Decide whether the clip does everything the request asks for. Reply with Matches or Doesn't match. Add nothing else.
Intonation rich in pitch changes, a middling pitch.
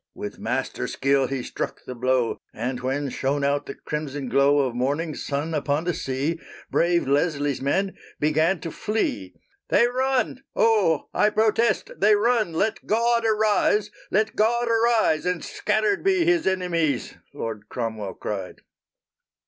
Matches